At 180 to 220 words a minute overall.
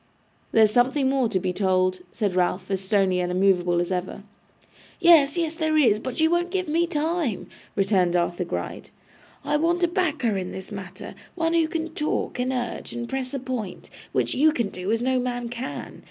Yes: average, 195 wpm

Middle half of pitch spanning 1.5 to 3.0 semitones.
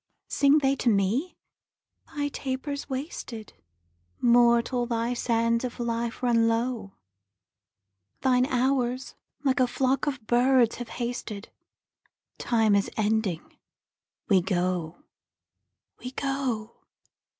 Yes: narrow, 2.4 semitones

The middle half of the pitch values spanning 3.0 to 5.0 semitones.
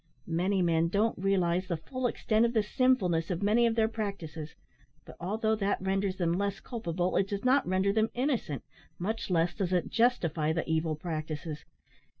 Yes: average, 4.5 semitones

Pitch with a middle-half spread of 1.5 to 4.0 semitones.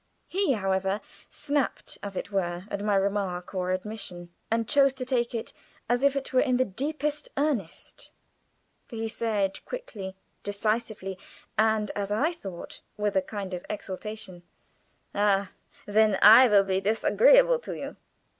No: average, 4.7 semitones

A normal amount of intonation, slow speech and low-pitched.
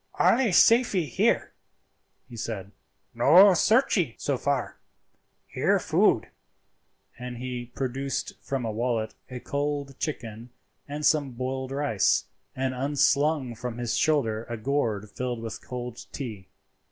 Yes: average, 3.5 semitones; slow, 125 wpm; low, 130 Hz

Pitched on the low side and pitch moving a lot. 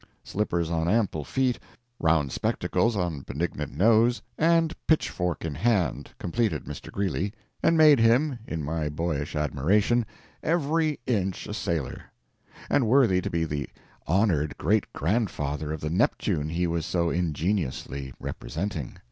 Yes: very low, 90 Hz; wide, 6.8 semitones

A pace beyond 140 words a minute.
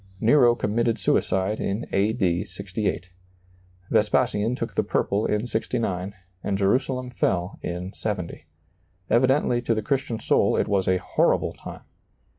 No: slow, 135 wpm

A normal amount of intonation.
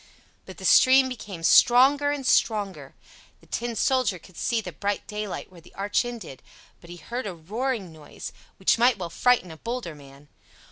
No: wide, 6.4 semitones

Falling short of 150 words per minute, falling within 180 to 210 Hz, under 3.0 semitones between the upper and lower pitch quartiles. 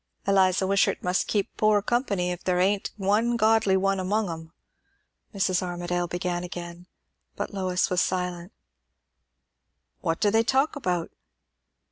Yes: slow, 135 wpm; medium, 185 Hz; narrow, 2.5 semitones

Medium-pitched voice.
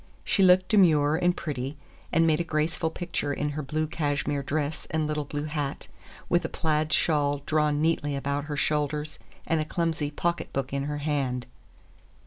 Yes: medium, 150 Hz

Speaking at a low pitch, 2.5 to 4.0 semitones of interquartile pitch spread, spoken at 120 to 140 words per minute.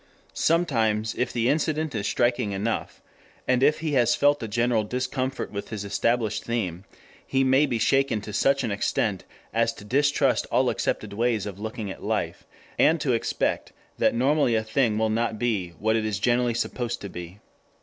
No: low, 115 Hz; average, 3.5 semitones; average, 180 wpm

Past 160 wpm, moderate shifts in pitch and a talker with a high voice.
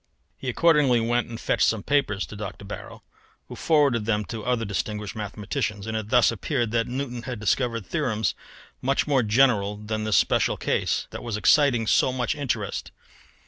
No: average, 175 wpm; average, 3.2 semitones; low, 115 Hz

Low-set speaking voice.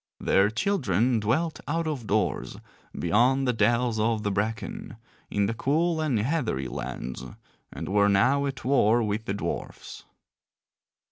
Yes: low, 115 Hz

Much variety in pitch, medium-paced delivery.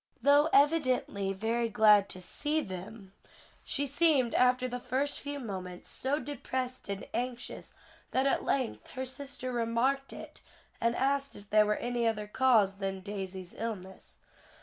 No: average, 4.7 semitones; average, 150 wpm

